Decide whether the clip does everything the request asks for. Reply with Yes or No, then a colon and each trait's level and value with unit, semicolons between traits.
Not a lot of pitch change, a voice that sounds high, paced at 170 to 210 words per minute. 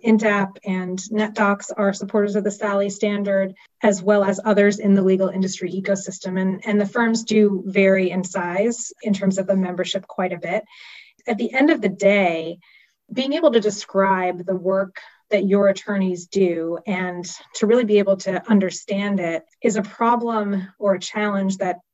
Yes: narrow, 2.0 semitones; high, 200 Hz; average, 180 wpm